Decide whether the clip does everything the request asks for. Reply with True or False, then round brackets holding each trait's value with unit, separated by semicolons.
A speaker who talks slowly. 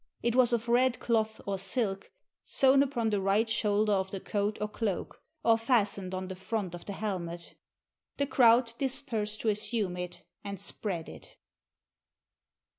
False (165 wpm)